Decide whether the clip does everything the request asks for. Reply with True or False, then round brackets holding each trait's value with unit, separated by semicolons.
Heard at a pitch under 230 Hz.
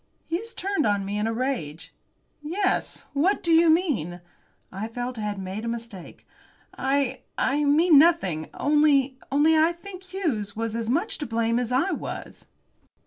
False (270 Hz)